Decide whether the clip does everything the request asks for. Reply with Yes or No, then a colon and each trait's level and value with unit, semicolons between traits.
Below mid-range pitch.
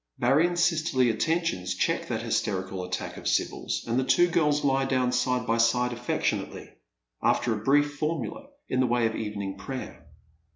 Yes: low, 125 Hz